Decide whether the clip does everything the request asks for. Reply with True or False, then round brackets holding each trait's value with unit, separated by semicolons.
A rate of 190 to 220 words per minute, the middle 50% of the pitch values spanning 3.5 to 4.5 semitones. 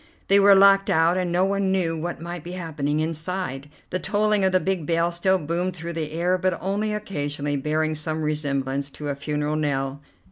True (200 wpm; 3.8 semitones)